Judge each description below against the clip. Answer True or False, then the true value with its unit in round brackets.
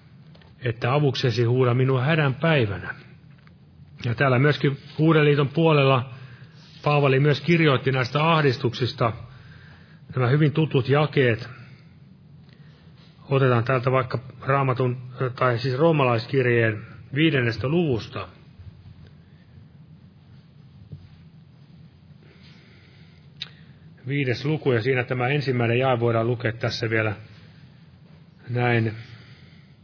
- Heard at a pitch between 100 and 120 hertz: False (135 Hz)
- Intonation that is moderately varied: True (3.4 semitones)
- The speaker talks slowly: True (80 wpm)